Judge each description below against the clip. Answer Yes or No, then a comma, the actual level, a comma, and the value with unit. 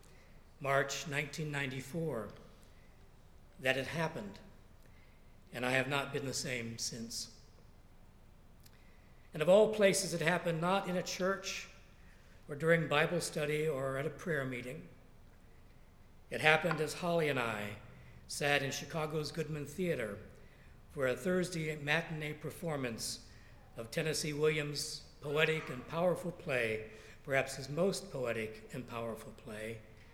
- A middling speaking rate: No, slow, 125 wpm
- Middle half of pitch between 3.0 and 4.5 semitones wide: No, average, 5.1 semitones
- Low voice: No, medium, 145 Hz